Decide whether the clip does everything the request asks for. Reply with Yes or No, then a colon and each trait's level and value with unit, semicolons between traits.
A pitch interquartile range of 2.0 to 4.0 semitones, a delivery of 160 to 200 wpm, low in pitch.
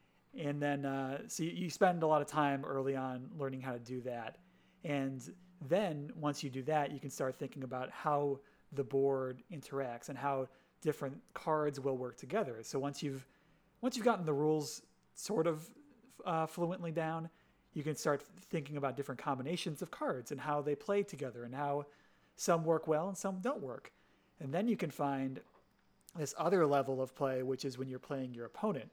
No: average, 3.4 semitones; average, 190 wpm; medium, 145 Hz